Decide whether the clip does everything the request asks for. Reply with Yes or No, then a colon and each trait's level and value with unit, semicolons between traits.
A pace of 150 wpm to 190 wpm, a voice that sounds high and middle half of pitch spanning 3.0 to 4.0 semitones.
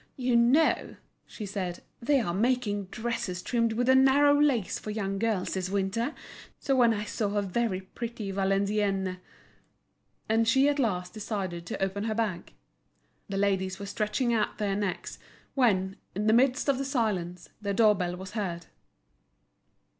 Yes: average, 160 wpm; high, 210 Hz; average, 3.6 semitones